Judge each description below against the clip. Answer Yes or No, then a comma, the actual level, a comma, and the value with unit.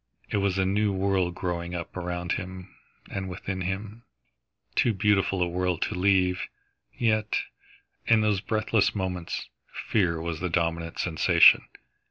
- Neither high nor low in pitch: No, very low, 95 Hz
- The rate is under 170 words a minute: Yes, average, 140 wpm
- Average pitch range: No, narrow, 2.2 semitones